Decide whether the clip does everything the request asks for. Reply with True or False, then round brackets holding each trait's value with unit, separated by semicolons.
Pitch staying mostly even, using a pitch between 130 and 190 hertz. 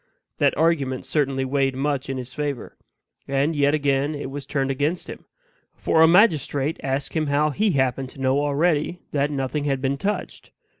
True (2.1 semitones; 140 Hz)